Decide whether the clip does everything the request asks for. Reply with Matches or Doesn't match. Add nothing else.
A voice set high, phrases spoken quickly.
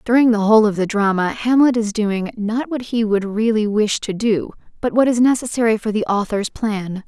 Matches